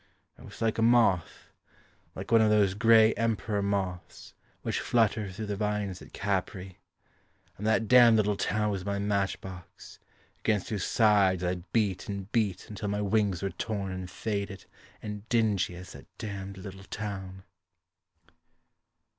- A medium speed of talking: Yes, average, 155 wpm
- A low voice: Yes, low, 100 Hz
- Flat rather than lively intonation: Yes, narrow, 2.2 semitones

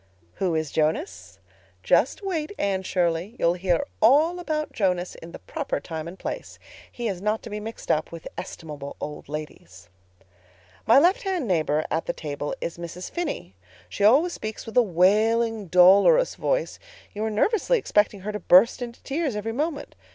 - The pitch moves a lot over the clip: Yes, wide, 8.2 semitones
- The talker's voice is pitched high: Yes, high, 210 Hz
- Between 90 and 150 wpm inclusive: No, average, 170 wpm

